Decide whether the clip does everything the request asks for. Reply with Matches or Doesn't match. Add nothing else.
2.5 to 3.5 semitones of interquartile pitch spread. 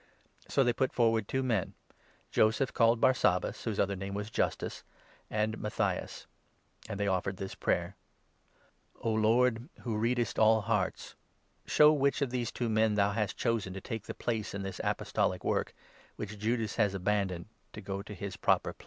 Matches